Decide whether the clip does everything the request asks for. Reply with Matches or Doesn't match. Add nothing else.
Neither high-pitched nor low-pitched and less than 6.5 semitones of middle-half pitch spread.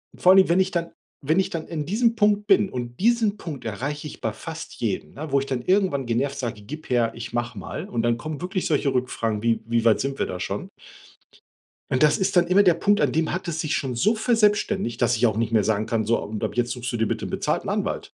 Doesn't match